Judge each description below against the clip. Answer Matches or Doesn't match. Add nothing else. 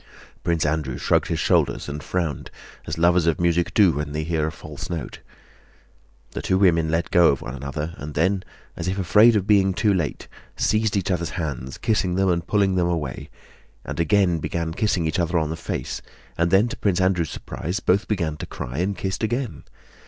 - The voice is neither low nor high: Doesn't match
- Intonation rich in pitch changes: Doesn't match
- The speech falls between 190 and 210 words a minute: Matches